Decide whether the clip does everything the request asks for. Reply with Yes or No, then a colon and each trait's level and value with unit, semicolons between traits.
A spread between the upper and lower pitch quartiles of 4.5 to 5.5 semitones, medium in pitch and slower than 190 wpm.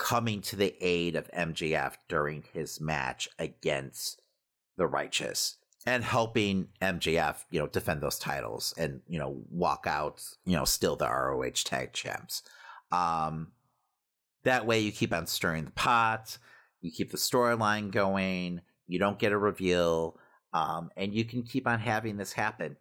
No: average, 4.9 semitones; low, 100 Hz; average, 160 wpm